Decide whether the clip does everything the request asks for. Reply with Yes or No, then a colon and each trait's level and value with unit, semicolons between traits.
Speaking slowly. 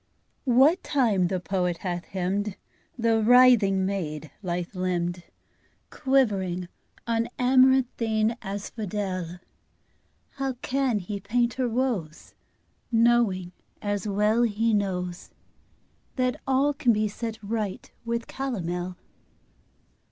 Yes: slow, 100 wpm